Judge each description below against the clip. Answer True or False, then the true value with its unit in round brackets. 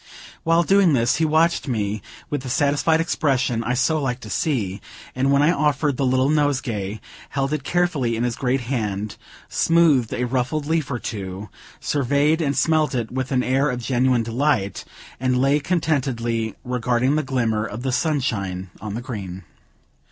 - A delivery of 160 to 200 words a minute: True (170 wpm)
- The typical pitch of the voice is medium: False (130 Hz)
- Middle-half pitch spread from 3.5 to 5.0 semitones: True (4.2 semitones)